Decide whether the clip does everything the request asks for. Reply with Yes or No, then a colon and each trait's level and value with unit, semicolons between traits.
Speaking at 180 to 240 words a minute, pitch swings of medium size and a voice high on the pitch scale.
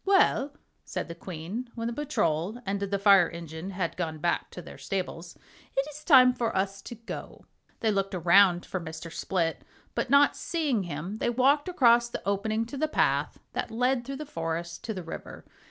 No: average, 190 wpm; wide, 6.3 semitones; high, 200 Hz